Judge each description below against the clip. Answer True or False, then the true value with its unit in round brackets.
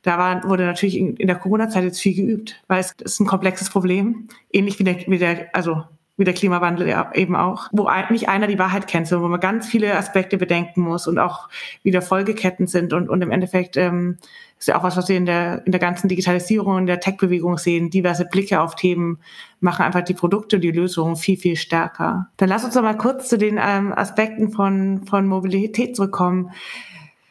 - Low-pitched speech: False (185 Hz)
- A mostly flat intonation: True (2.1 semitones)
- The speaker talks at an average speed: False (205 wpm)